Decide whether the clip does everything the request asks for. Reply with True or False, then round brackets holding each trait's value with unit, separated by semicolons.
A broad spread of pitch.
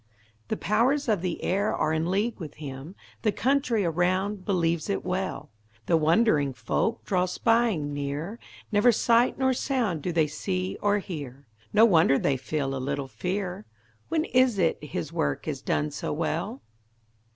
True (6.1 semitones)